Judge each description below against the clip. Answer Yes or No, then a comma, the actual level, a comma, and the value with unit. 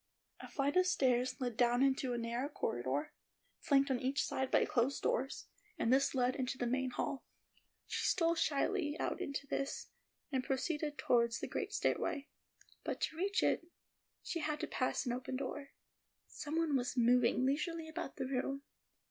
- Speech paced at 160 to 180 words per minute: Yes, average, 175 wpm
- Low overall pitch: No, very high, 270 Hz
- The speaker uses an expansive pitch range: No, average, 2.8 semitones